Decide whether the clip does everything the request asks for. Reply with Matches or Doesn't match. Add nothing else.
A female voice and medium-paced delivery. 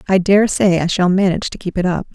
Doesn't match